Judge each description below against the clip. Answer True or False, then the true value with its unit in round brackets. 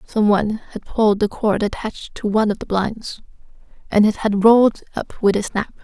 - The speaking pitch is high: True (210 Hz)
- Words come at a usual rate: True (195 wpm)